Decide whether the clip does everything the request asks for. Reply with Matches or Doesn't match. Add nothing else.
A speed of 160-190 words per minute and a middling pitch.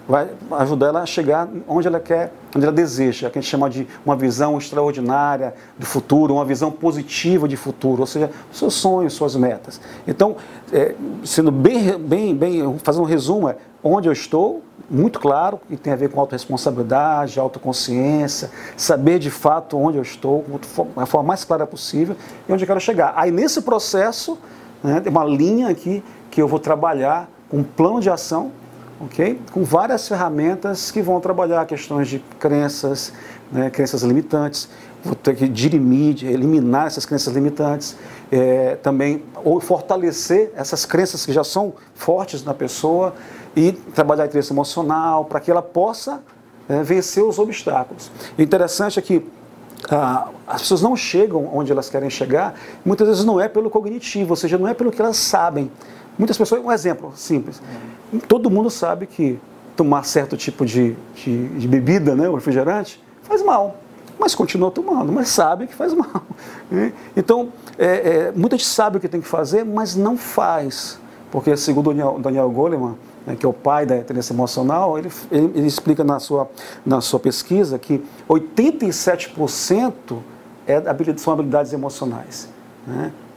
Matches